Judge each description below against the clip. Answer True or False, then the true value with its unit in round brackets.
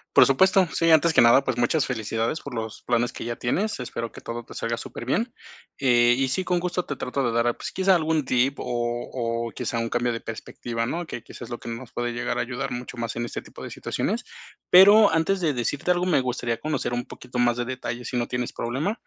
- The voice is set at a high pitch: False (125 Hz)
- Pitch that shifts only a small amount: False (5.1 semitones)